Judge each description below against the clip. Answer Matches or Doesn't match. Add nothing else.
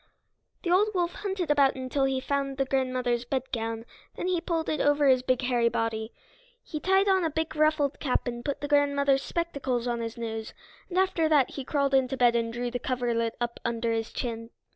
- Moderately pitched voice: Doesn't match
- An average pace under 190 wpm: Doesn't match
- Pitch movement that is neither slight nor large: Matches